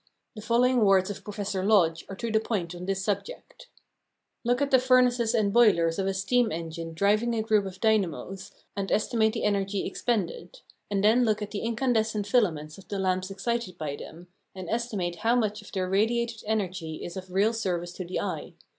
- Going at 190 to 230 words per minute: Yes, average, 195 wpm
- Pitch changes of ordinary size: Yes, average, 3.6 semitones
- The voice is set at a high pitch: Yes, high, 205 Hz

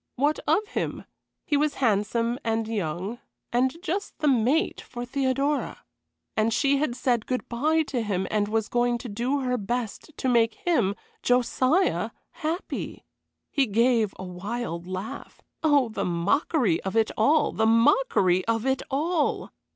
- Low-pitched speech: No, high, 240 Hz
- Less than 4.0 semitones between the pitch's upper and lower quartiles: No, average, 4.6 semitones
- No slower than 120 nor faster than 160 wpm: Yes, average, 150 wpm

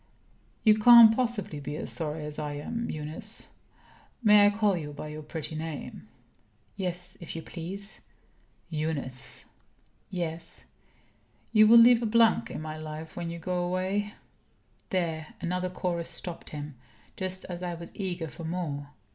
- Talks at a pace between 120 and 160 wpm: Yes, average, 155 wpm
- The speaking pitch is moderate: Yes, medium, 175 Hz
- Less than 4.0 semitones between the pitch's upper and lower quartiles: No, average, 4.3 semitones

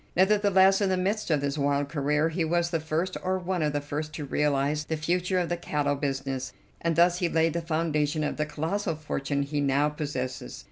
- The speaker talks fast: Yes, fast, 215 wpm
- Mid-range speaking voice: Yes, medium, 155 Hz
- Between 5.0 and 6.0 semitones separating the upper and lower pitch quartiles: No, average, 3.2 semitones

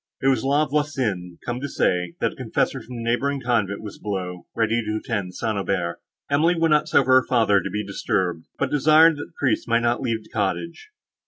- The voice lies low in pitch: Yes, low, 115 Hz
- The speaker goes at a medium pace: No, fast, 215 wpm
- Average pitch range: No, wide, 6.0 semitones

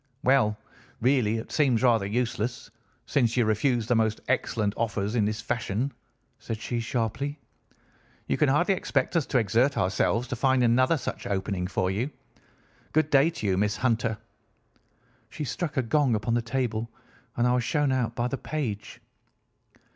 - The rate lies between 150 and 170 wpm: Yes, average, 165 wpm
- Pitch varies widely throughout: No, average, 3.4 semitones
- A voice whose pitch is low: Yes, low, 120 Hz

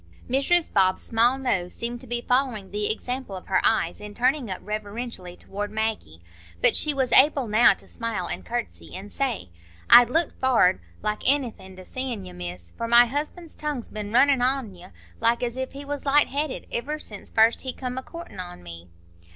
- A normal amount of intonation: Yes, average, 4.6 semitones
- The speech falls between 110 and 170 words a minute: No, average, 195 wpm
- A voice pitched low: No, high, 235 Hz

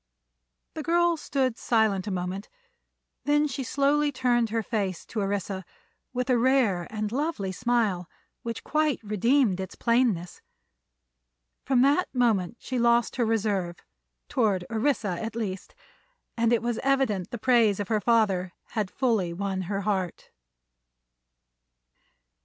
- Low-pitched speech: No, high, 225 Hz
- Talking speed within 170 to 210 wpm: No, slow, 135 wpm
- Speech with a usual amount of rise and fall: Yes, average, 4.4 semitones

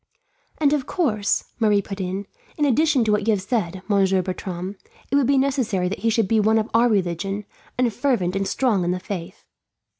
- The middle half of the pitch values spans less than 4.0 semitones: No, average, 4.3 semitones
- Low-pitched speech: No, high, 210 Hz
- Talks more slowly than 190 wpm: No, fast, 205 wpm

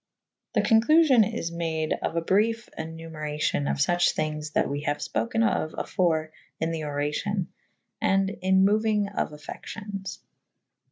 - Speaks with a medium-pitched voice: Yes, medium, 170 Hz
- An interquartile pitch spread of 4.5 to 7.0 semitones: Yes, average, 5.0 semitones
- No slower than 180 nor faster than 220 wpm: No, slow, 135 wpm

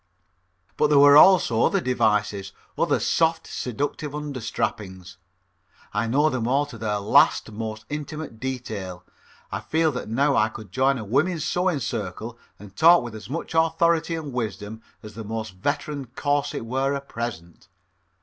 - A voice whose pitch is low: Yes, low, 125 Hz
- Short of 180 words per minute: Yes, average, 155 wpm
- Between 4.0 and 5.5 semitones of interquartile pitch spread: Yes, average, 5.1 semitones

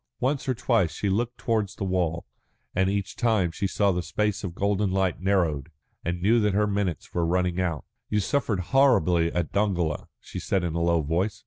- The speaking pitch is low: Yes, very low, 95 Hz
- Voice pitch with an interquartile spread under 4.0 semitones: Yes, average, 3.4 semitones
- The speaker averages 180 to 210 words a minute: Yes, average, 200 wpm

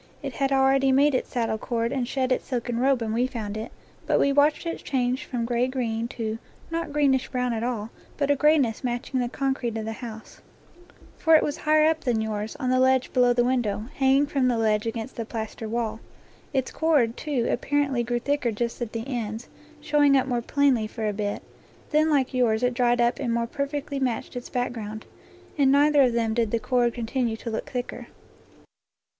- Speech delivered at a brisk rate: Yes, fast, 210 wpm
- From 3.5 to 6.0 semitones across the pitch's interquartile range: No, average, 3.0 semitones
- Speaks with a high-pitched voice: Yes, high, 245 Hz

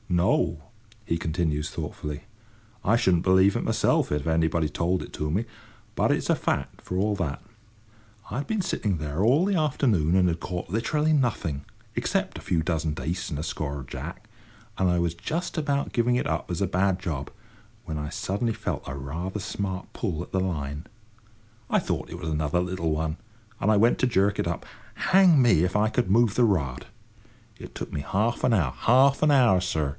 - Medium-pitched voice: No, very low, 90 Hz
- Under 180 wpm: No, average, 195 wpm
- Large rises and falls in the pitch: Yes, wide, 6.2 semitones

